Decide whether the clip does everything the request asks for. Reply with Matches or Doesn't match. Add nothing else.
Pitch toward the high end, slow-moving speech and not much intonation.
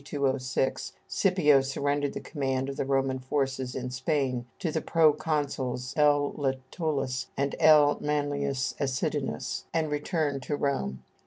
Doesn't match